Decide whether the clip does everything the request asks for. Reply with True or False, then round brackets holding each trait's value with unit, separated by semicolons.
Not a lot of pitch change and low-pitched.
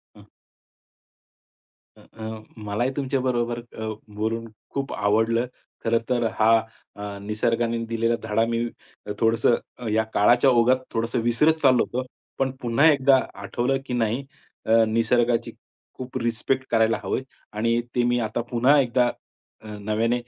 True (1.9 semitones; 115 Hz)